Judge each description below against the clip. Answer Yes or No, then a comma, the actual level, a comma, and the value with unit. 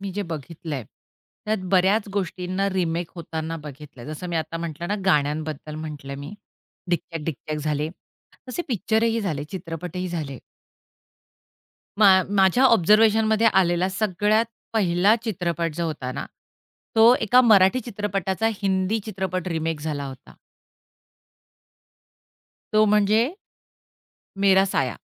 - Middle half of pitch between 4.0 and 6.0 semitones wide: Yes, average, 4.7 semitones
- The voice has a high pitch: No, medium, 180 Hz